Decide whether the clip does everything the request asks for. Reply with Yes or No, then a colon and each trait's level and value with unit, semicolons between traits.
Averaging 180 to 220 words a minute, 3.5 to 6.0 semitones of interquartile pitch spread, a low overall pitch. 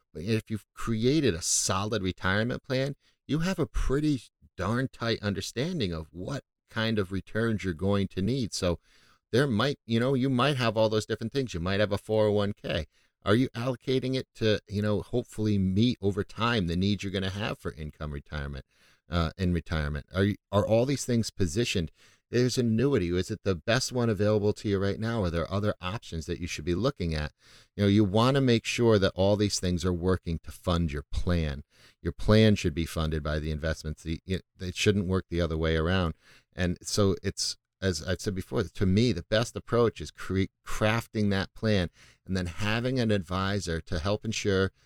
Yes: average, 200 wpm; average, 4.3 semitones; low, 100 Hz